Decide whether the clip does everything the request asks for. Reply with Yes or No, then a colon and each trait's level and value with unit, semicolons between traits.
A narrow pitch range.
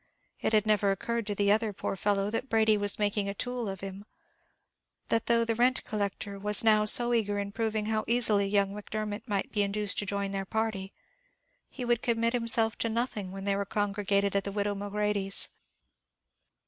Yes: narrow, 2.0 semitones